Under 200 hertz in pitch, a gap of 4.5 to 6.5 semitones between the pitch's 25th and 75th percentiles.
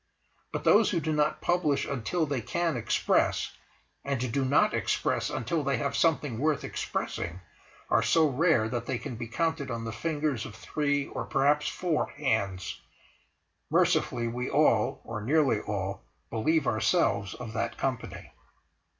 Yes: low, 135 Hz; average, 5.2 semitones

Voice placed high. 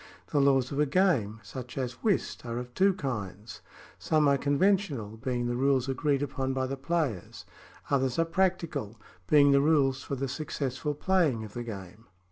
No: low, 135 Hz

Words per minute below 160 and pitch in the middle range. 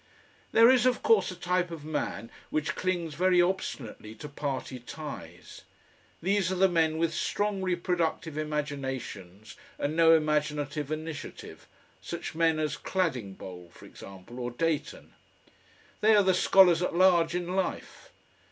Yes: average, 140 wpm; medium, 160 Hz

